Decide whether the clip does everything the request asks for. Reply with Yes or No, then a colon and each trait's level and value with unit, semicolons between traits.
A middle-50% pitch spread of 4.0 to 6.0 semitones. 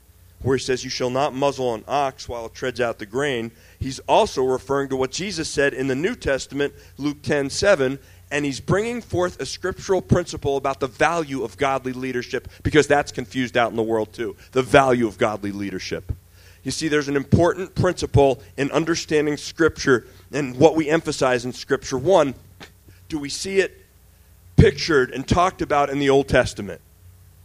Yes: average, 5.0 semitones